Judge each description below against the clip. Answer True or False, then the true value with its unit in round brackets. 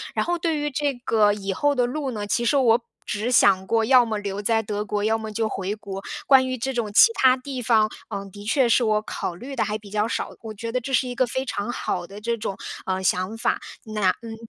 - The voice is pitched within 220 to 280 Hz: True (225 Hz)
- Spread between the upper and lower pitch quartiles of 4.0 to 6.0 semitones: False (3.6 semitones)